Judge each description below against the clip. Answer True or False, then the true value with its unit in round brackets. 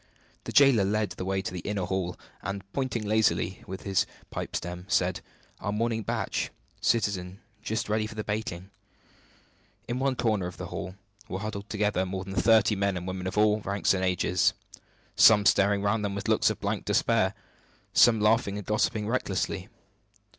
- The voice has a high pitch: False (100 Hz)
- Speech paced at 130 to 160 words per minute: False (175 wpm)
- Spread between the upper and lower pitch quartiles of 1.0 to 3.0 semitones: True (2.4 semitones)